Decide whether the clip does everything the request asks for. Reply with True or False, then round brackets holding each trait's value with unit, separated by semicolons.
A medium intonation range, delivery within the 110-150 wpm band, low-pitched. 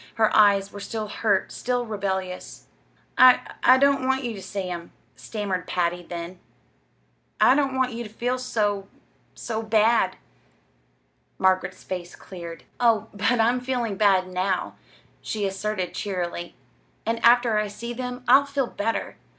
False (4.3 semitones; 145 wpm; 215 Hz)